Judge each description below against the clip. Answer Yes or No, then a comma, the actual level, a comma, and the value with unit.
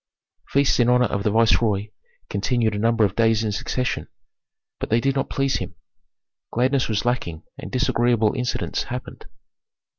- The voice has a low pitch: Yes, low, 115 Hz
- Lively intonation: No, average, 2.8 semitones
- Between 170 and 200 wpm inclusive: No, average, 155 wpm